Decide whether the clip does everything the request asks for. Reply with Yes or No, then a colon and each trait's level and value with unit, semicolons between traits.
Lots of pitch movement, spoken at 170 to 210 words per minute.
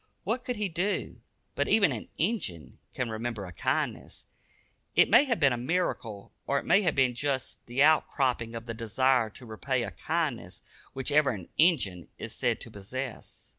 Yes: wide, 5.9 semitones; average, 185 wpm